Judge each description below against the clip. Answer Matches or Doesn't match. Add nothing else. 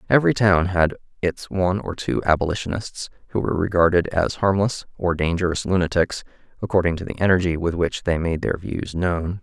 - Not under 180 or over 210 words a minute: Doesn't match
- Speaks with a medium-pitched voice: Doesn't match